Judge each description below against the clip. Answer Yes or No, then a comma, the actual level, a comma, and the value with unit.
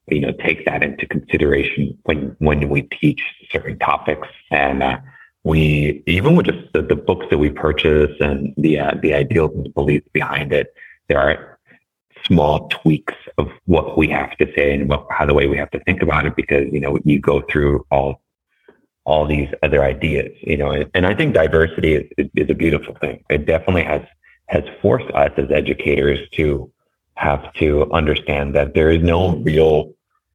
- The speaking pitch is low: Yes, very low, 75 Hz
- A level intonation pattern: Yes, narrow, 1.7 semitones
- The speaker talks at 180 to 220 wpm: Yes, average, 185 wpm